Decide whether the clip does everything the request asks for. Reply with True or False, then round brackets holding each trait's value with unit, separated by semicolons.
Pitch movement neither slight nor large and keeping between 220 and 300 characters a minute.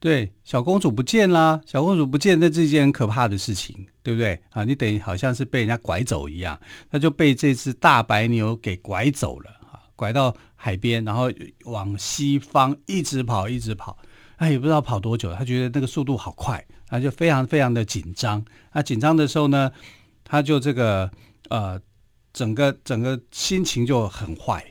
True (5.0 semitones; 275 characters per minute)